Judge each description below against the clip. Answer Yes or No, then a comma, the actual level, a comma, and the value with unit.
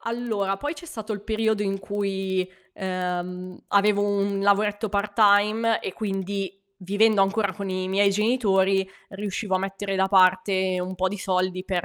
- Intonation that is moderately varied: No, narrow, 1.7 semitones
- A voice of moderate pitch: No, high, 195 Hz